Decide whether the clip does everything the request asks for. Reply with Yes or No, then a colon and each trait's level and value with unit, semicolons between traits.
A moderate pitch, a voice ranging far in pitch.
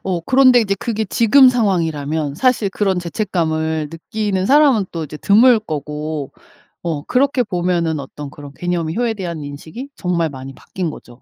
Yes: medium, 175 Hz; wide, 5.9 semitones